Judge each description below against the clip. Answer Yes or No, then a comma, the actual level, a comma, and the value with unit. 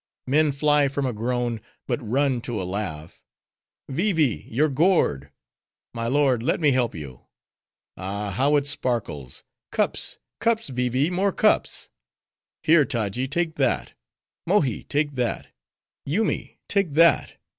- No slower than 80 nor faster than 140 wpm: Yes, slow, 135 wpm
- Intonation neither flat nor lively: Yes, average, 4.8 semitones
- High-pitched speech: No, low, 135 Hz